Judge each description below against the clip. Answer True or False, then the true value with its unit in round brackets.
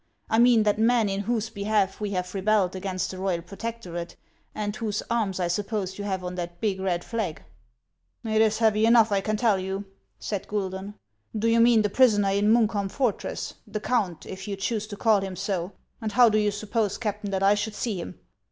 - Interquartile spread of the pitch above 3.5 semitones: False (2.4 semitones)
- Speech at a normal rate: False (220 wpm)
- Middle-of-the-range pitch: False (205 Hz)